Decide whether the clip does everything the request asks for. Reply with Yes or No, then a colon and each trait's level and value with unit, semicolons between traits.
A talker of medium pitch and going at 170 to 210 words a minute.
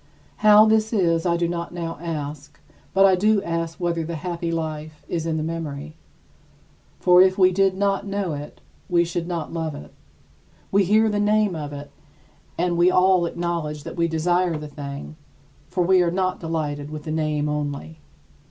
Yes: medium, 170 Hz; average, 180 wpm